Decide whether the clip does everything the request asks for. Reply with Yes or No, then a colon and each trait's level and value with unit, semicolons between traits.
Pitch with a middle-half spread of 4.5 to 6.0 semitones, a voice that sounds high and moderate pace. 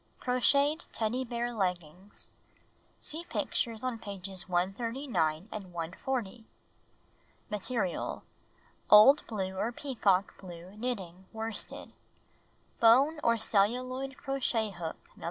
No: average, 5.1 semitones; high, 220 Hz; slow, 100 wpm